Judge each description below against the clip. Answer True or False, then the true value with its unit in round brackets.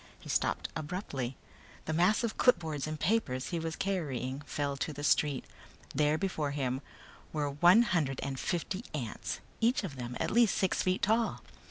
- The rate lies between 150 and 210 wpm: True (170 wpm)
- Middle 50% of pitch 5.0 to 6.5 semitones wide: True (5.3 semitones)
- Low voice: False (155 Hz)